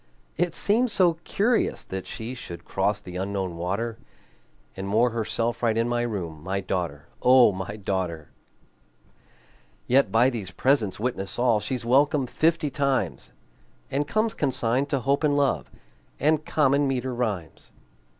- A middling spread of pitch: No, wide, 6.2 semitones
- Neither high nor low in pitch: No, low, 120 Hz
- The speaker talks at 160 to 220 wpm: No, average, 145 wpm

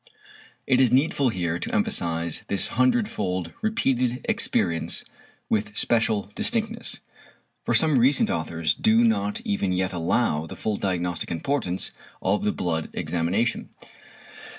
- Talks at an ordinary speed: No, slow, 125 wpm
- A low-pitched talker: Yes, low, 105 Hz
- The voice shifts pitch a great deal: Yes, wide, 6.5 semitones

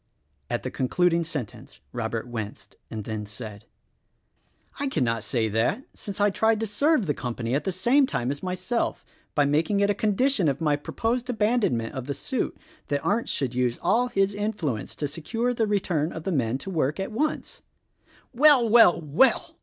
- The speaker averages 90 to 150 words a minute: No, average, 185 wpm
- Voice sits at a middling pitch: Yes, medium, 170 Hz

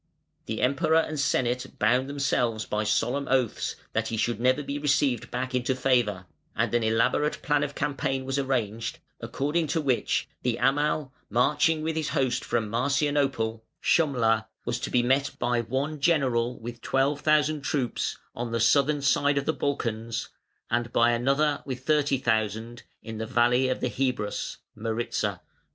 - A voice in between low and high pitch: No, low, 130 Hz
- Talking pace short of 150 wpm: No, average, 160 wpm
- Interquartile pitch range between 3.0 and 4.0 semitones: Yes, average, 3.3 semitones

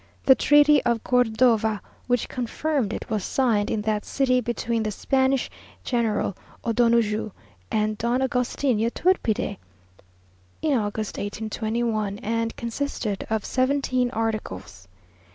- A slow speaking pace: Yes, slow, 115 wpm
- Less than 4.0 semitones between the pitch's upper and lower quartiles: Yes, average, 2.8 semitones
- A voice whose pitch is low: No, high, 230 Hz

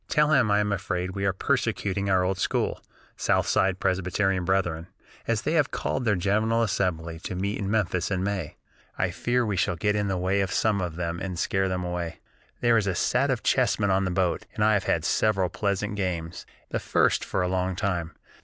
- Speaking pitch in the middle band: No, very low, 95 Hz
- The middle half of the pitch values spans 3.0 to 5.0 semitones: No, narrow, 2.5 semitones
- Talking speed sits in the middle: No, fast, 210 wpm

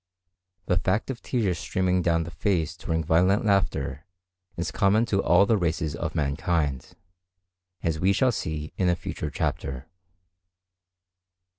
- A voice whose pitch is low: Yes, very low, 85 Hz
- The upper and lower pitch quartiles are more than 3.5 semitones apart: Yes, average, 3.9 semitones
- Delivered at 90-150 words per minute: Yes, average, 140 wpm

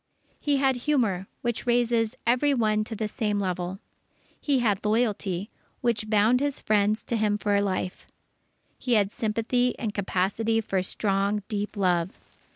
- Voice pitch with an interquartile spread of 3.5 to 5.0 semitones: No, average, 3.0 semitones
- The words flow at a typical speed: Yes, average, 150 wpm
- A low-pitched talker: No, high, 215 Hz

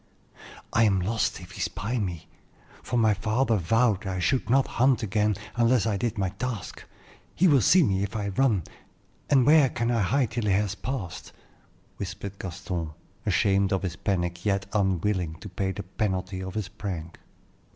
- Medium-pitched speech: No, low, 100 Hz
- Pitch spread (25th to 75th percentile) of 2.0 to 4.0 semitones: Yes, average, 3.6 semitones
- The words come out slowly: No, average, 175 wpm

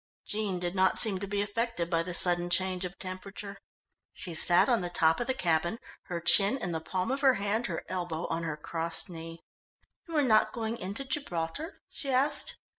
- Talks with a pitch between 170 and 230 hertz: Yes, medium, 185 Hz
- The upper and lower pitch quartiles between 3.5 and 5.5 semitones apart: Yes, average, 4.6 semitones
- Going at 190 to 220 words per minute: Yes, average, 200 wpm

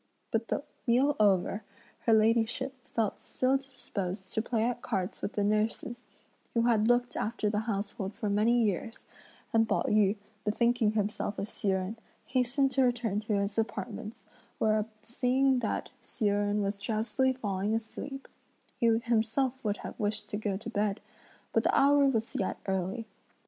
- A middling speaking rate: Yes, average, 160 wpm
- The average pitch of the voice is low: No, high, 220 Hz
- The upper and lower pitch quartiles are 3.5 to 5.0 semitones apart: No, average, 2.7 semitones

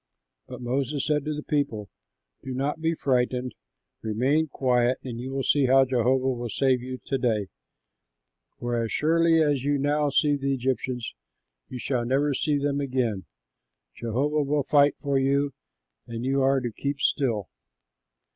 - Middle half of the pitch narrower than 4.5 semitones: Yes, narrow, 2.6 semitones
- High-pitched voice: No, low, 135 Hz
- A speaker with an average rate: Yes, average, 165 wpm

